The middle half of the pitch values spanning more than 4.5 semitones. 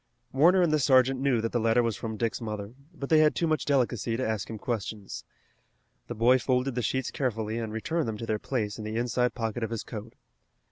No: average, 3.0 semitones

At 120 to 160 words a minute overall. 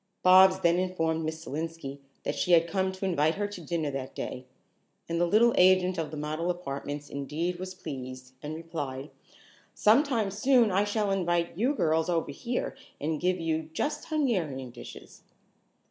No: average, 170 wpm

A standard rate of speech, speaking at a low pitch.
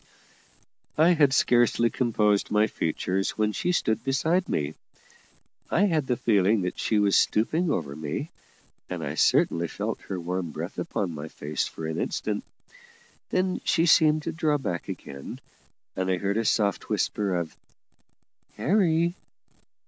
Yes: average, 150 wpm; low, 110 Hz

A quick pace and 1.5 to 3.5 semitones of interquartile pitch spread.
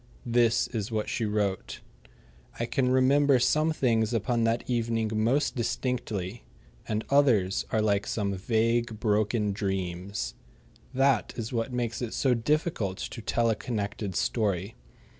No: average, 140 wpm; average, 2.9 semitones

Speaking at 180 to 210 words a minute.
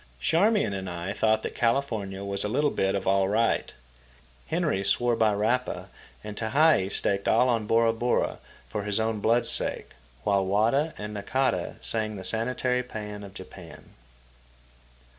No: average, 155 wpm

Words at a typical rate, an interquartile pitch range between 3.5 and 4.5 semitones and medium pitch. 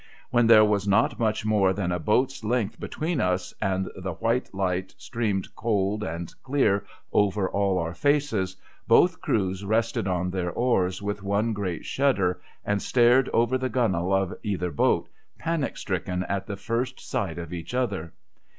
No: average, 165 wpm; average, 3.9 semitones; low, 100 Hz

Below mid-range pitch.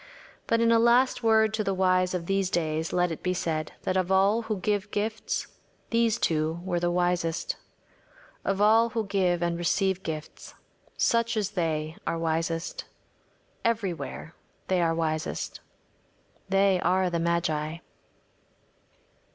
No: medium, 185 Hz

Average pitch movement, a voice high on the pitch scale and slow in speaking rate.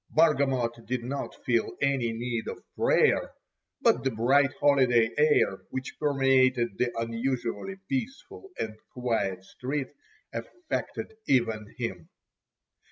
No: average, 3.1 semitones; low, 125 Hz; slow, 110 wpm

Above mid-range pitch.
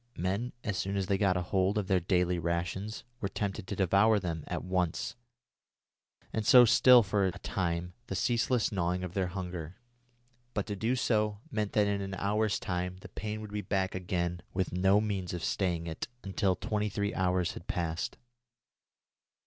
No: very low, 95 Hz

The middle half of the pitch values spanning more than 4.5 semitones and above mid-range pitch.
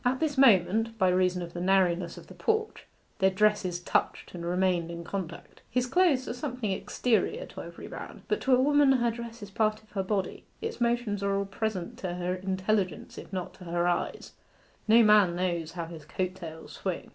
Yes: average, 4.9 semitones; high, 195 Hz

